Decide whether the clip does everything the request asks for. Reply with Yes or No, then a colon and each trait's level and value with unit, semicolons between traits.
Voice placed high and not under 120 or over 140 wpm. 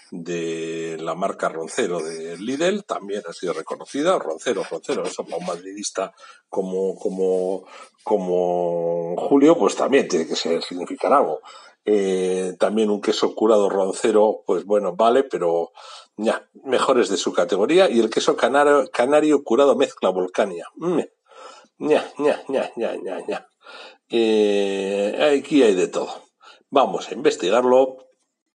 No: low, 105 Hz; slow, 125 wpm